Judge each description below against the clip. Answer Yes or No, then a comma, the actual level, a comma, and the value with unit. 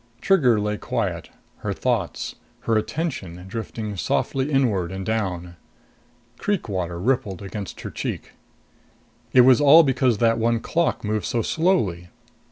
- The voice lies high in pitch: No, low, 110 Hz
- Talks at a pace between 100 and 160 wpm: Yes, slow, 135 wpm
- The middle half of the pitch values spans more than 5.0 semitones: Yes, wide, 5.6 semitones